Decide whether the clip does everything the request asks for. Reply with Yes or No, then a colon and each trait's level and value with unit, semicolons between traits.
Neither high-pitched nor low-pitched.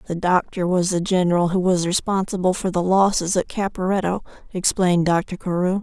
Yes: medium, 180 Hz